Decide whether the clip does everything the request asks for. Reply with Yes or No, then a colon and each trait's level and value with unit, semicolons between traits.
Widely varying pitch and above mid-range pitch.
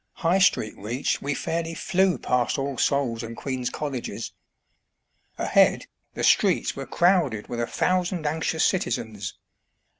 No: wide, 6.1 semitones; medium, 140 Hz